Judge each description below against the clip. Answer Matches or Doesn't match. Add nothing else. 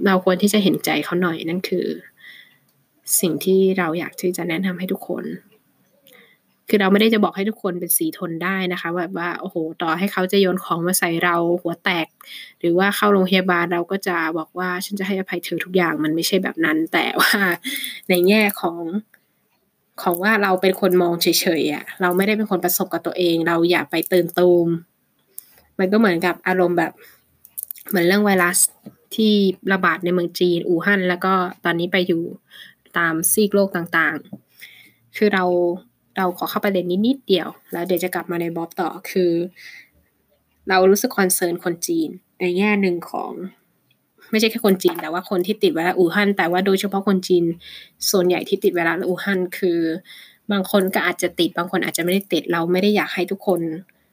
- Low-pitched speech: Doesn't match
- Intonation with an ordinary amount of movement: Doesn't match